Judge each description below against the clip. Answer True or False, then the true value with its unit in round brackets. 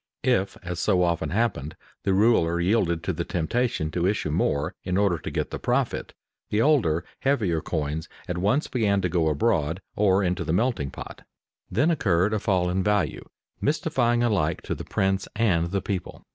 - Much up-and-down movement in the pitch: False (4.4 semitones)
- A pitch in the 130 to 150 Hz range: False (95 Hz)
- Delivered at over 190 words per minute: False (180 wpm)